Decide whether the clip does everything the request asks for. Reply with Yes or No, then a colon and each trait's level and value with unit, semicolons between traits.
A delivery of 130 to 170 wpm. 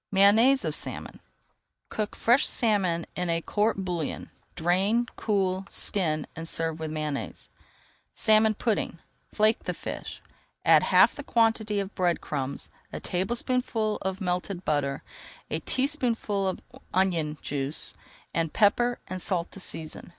Yes: slow, 135 wpm